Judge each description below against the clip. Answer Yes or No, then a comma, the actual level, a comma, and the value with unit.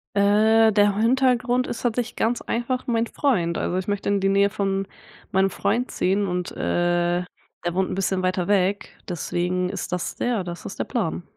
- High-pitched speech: Yes, high, 200 Hz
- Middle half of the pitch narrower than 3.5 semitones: No, average, 3.8 semitones